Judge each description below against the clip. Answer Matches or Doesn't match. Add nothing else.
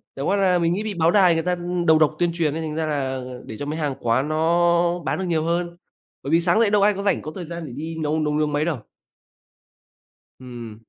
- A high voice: Doesn't match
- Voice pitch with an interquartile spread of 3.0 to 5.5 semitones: Doesn't match